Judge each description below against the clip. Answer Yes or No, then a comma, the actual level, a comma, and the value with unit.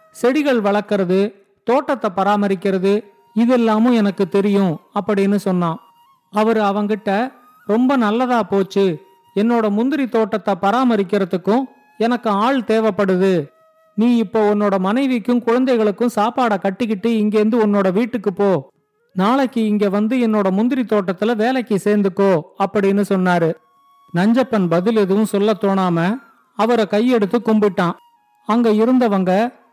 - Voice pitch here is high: Yes, high, 210 Hz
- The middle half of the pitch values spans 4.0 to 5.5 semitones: No, average, 3.2 semitones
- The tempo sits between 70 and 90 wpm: No, average, 105 wpm